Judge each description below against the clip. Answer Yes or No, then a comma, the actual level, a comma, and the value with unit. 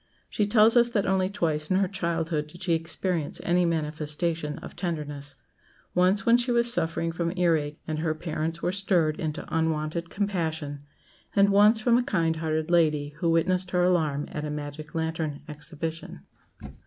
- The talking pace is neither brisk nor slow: Yes, average, 170 wpm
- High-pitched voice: No, medium, 165 Hz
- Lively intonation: No, average, 3.2 semitones